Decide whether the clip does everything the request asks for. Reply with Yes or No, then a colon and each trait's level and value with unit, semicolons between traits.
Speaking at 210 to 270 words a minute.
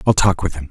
No: fast, 340 wpm